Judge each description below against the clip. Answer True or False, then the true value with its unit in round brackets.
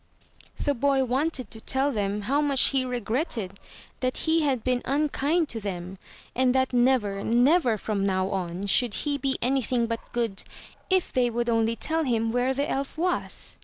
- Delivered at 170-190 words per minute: True (175 wpm)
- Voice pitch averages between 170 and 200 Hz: False (250 Hz)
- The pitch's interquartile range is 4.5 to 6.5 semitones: False (3.9 semitones)